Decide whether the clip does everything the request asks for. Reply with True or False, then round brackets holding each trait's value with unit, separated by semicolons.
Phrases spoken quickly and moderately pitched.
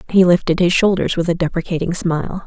False (195 wpm; 175 Hz)